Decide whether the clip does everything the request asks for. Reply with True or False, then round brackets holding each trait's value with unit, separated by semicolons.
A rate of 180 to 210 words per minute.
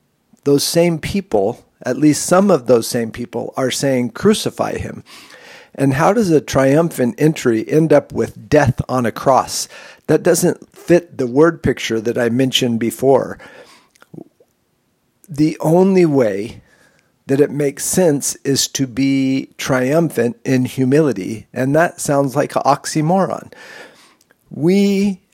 False (135 wpm)